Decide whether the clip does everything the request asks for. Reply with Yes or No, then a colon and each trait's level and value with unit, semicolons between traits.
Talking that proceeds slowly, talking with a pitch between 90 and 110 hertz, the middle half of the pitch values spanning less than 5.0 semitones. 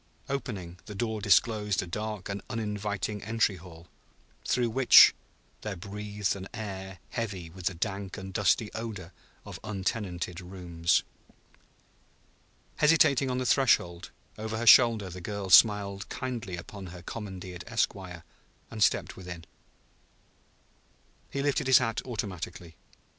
Yes: slow, 125 wpm; low, 100 Hz; average, 3.5 semitones